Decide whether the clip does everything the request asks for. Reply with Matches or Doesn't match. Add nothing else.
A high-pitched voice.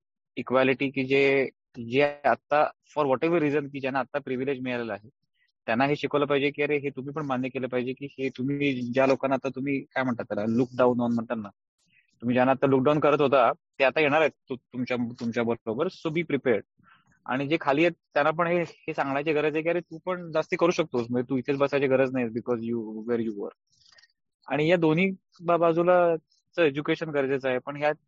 Doesn't match